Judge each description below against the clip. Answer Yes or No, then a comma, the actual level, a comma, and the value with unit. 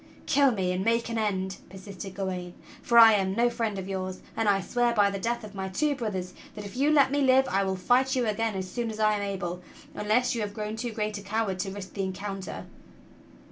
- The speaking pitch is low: No, high, 210 Hz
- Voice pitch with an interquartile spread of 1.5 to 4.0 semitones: Yes, average, 3.5 semitones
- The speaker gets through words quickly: Yes, fast, 240 wpm